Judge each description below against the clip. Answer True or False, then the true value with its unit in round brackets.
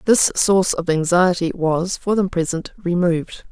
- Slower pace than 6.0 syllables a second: True (4.7 syllables/s)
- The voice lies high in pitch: False (175 Hz)